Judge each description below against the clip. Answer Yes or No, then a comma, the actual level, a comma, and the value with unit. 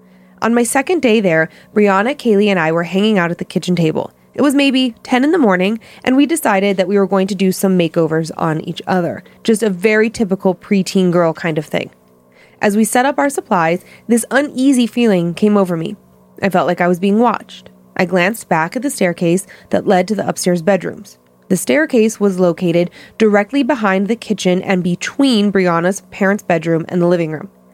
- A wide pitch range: No, average, 4.3 semitones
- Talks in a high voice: Yes, high, 195 Hz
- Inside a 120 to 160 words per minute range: No, fast, 205 wpm